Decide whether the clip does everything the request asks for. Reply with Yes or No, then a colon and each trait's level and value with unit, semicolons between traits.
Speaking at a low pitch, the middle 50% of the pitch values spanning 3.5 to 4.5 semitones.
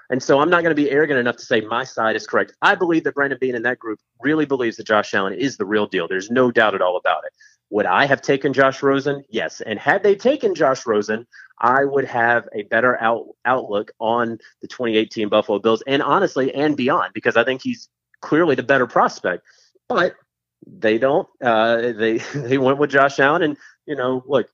Yes: low, 130 Hz; average, 4.1 semitones